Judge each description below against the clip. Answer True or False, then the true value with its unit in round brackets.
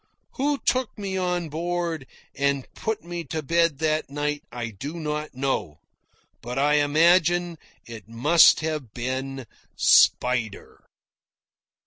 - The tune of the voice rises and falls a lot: False (4.3 semitones)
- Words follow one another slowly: True (120 wpm)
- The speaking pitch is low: False (150 Hz)